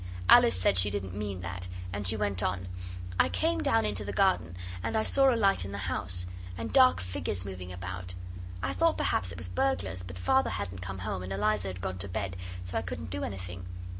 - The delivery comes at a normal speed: No, fast, 220 wpm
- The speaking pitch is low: Yes, very low, 95 Hz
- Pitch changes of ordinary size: No, narrow, 2.0 semitones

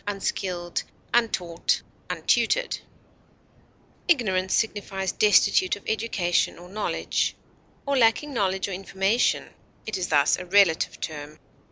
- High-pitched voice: Yes, high, 195 Hz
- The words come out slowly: Yes, slow, 110 wpm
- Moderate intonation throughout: Yes, average, 3.5 semitones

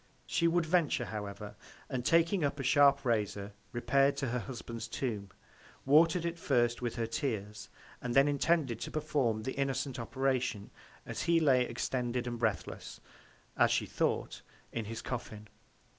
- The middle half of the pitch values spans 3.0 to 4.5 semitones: Yes, average, 3.8 semitones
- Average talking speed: Yes, average, 150 wpm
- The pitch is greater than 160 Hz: No, low, 125 Hz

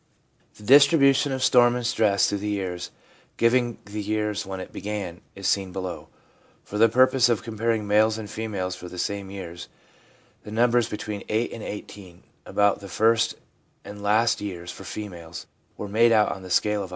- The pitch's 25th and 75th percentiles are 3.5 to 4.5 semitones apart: No, average, 2.8 semitones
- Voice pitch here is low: Yes, low, 105 Hz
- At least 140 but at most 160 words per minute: No, average, 190 wpm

